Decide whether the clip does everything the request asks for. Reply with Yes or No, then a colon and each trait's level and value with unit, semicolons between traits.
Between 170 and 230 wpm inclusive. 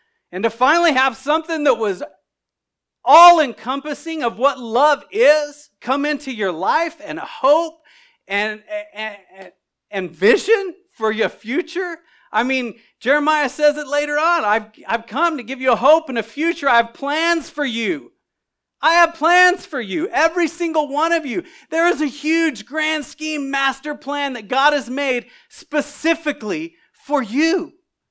No: average, 160 wpm